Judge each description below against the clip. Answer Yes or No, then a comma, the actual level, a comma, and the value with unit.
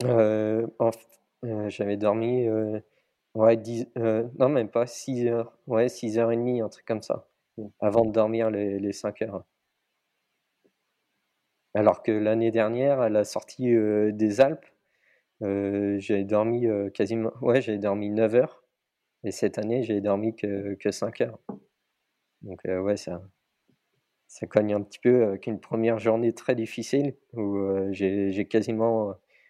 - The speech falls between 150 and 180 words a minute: Yes, average, 160 wpm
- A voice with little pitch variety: Yes, narrow, 2.2 semitones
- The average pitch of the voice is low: Yes, low, 110 Hz